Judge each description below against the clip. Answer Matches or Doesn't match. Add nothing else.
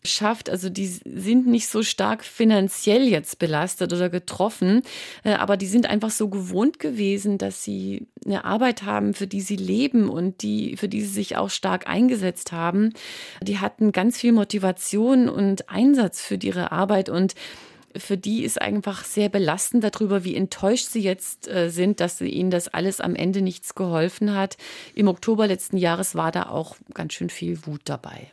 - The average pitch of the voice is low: Doesn't match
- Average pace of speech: Matches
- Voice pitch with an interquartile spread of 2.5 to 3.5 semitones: Matches